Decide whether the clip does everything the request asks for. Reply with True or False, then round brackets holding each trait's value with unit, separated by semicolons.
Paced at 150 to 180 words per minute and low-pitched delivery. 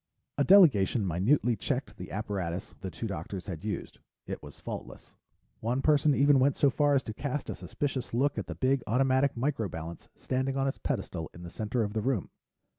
False (195 wpm; 125 Hz)